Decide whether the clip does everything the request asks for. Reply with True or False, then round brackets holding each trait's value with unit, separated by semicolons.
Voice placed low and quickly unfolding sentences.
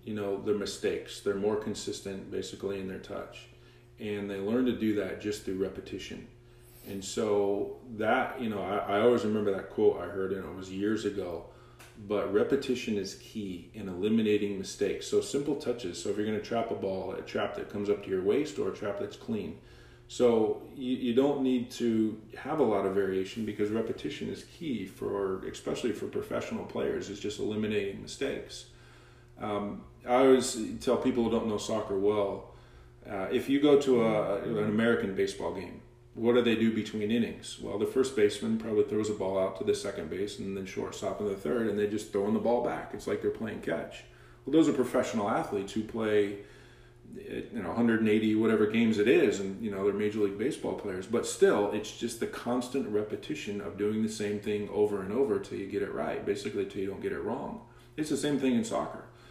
True (105 Hz; 210 wpm)